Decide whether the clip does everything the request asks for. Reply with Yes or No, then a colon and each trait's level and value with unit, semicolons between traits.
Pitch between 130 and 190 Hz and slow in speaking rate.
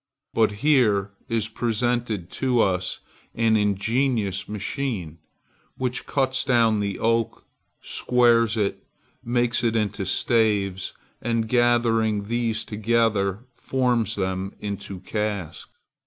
No: low, 110 Hz; slow, 105 wpm